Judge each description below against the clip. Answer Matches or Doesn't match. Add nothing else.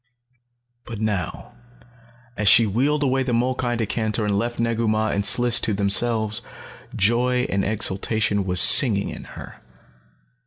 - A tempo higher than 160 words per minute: Doesn't match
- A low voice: Matches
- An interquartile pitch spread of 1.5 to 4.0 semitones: Matches